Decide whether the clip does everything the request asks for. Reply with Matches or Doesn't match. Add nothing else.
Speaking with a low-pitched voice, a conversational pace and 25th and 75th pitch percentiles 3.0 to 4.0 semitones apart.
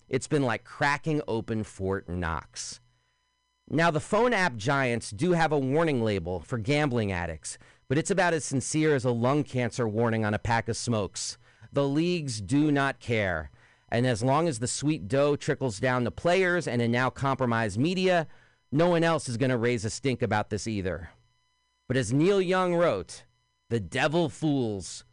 Doesn't match